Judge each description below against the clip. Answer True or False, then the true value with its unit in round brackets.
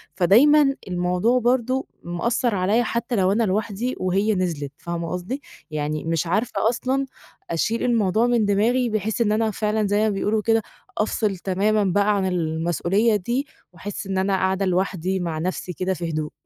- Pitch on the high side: True (200 Hz)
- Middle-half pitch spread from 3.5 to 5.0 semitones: True (4.0 semitones)